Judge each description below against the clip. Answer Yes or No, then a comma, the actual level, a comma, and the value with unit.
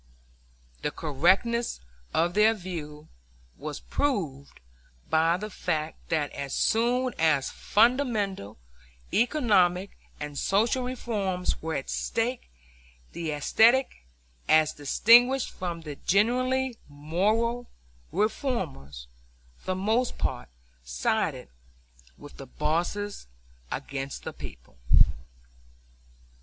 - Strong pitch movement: Yes, wide, 7.6 semitones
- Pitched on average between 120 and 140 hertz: No, medium, 185 Hz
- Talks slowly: Yes, slow, 95 wpm